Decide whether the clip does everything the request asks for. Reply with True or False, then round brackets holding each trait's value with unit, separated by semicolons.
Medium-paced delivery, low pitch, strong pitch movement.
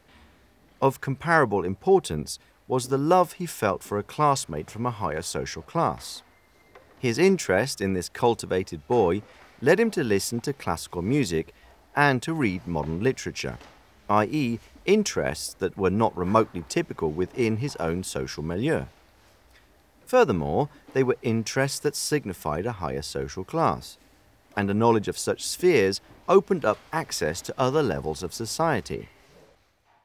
True (140 wpm; 110 Hz; 7.5 semitones)